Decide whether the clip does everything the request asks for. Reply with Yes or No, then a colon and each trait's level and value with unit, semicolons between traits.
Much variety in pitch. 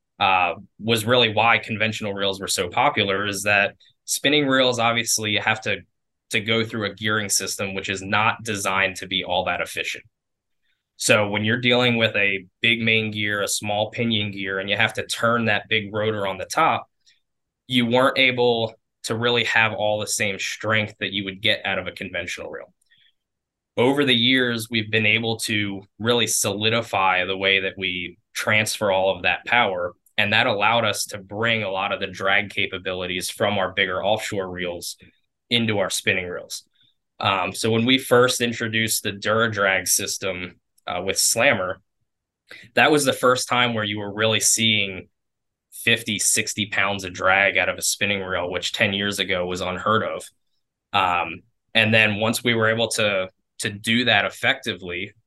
No: average, 2.9 semitones